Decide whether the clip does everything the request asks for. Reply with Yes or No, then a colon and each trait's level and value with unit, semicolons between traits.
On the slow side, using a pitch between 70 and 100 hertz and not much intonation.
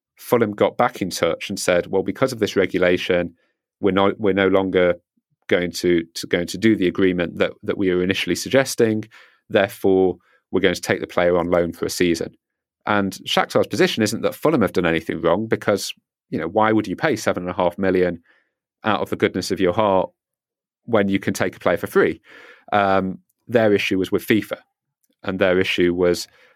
No: fast, 205 wpm; very low, 95 Hz; narrow, 2.2 semitones